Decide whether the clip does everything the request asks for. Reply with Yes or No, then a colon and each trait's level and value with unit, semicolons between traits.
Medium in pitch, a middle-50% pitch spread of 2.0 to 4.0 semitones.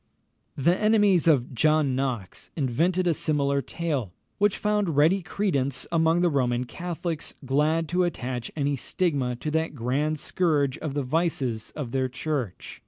No: medium, 150 Hz; average, 4.5 semitones